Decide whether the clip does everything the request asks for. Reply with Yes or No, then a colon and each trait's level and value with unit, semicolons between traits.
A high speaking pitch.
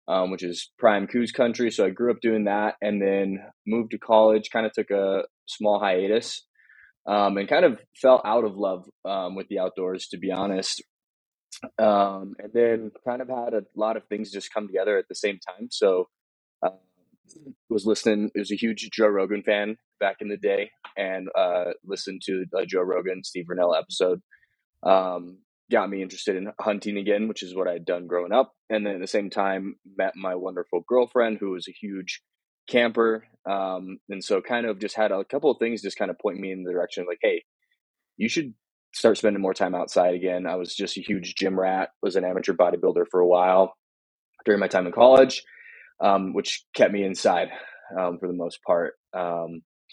No: low, 100 Hz